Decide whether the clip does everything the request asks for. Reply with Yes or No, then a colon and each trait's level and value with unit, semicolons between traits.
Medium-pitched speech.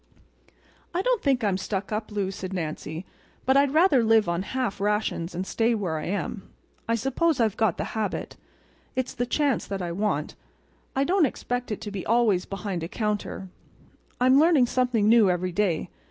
No: high, 215 Hz